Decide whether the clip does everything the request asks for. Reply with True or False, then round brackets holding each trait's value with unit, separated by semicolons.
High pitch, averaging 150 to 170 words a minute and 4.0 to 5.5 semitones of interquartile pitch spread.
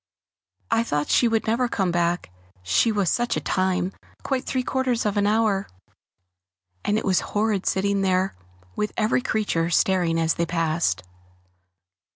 True (195 Hz; 160 wpm; 4.5 semitones)